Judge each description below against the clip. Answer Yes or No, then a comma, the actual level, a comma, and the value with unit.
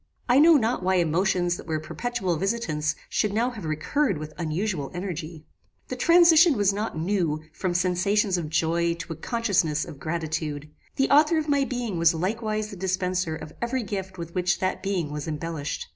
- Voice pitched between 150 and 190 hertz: Yes, medium, 185 Hz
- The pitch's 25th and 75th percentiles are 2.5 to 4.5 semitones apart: No, average, 5.2 semitones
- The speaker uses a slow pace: No, average, 180 wpm